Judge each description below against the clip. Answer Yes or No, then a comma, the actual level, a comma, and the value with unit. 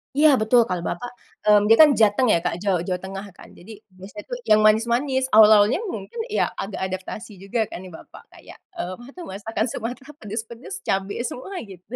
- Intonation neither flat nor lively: Yes, average, 4.0 semitones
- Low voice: No, high, 215 Hz